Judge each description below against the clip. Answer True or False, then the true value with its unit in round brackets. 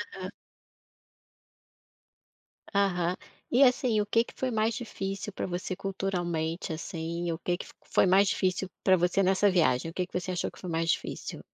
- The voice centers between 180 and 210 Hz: True (185 Hz)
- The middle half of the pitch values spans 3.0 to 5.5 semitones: False (2.4 semitones)